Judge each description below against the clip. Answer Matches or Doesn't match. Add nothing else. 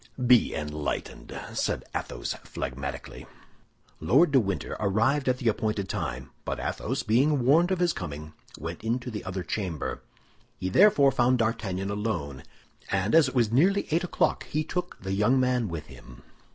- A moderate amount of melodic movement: Doesn't match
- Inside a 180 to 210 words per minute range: Doesn't match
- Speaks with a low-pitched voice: Matches